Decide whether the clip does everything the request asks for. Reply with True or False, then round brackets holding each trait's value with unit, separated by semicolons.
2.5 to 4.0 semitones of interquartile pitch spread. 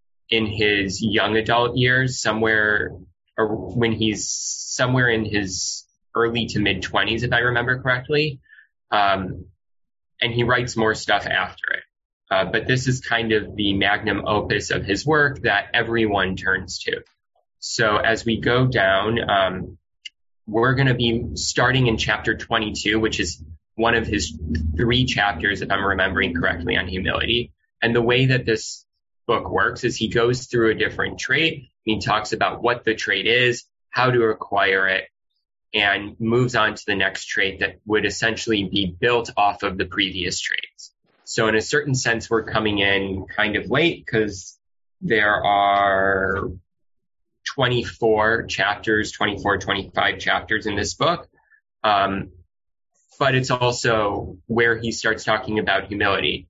True (3.2 semitones)